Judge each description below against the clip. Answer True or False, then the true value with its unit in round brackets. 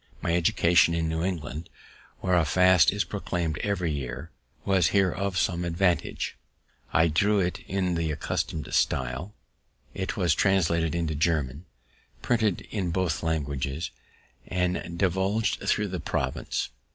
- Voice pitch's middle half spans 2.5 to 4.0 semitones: True (2.8 semitones)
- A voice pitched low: True (85 Hz)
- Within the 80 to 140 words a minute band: True (135 wpm)